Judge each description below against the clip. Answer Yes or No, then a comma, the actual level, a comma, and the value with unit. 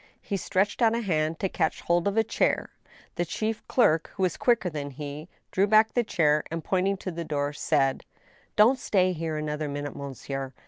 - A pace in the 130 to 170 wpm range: No, average, 195 wpm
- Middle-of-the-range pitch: Yes, medium, 170 Hz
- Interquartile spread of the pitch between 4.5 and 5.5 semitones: Yes, average, 5.1 semitones